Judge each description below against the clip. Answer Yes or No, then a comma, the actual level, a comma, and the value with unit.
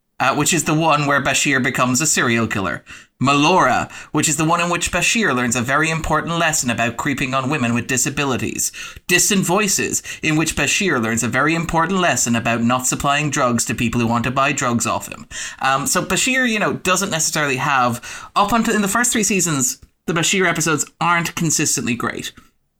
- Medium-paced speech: Yes, average, 195 wpm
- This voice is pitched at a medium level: Yes, medium, 150 Hz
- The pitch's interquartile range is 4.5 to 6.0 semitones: Yes, wide, 5.6 semitones